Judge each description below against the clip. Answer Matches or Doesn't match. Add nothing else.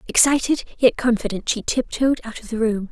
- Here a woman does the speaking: Matches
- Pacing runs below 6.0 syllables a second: Matches